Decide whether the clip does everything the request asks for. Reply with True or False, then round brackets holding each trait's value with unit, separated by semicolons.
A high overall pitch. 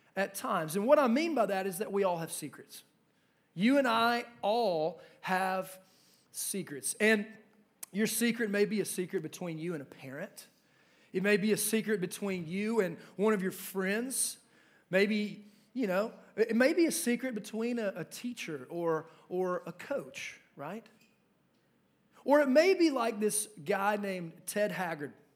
True (205 Hz)